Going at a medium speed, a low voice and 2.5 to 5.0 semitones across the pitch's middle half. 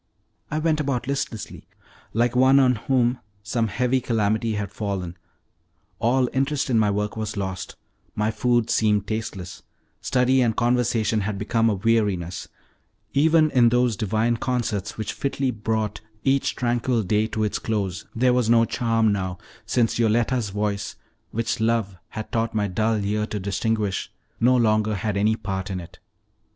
Yes: average, 155 wpm; low, 110 Hz; average, 2.9 semitones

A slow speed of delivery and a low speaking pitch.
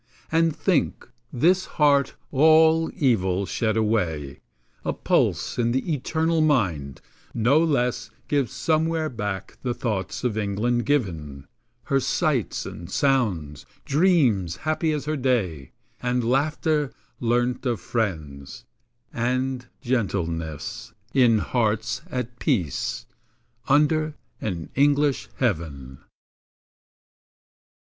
Yes: slow, 105 wpm; low, 125 Hz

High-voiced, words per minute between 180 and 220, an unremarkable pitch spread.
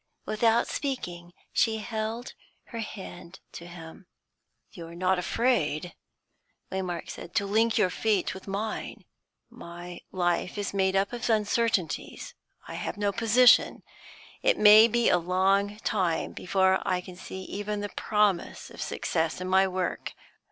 No: high, 195 Hz; average, 145 wpm; average, 3.3 semitones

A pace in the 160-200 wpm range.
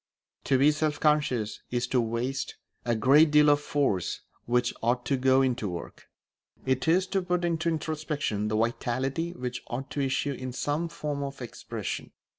Yes: average, 170 wpm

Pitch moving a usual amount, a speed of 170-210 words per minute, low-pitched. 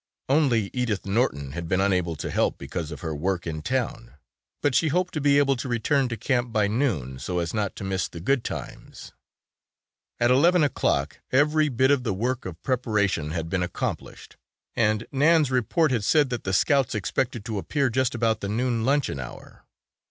No: wide, 6.1 semitones; average, 190 wpm; low, 115 Hz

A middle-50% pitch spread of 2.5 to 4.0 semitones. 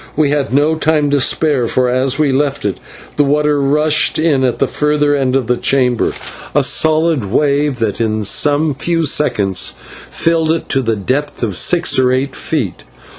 Yes: average, 3.0 semitones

